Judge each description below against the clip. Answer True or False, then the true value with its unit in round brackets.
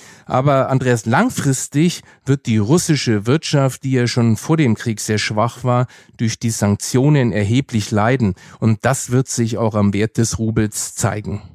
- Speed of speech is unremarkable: True (160 wpm)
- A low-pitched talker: True (120 Hz)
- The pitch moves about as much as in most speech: True (3.3 semitones)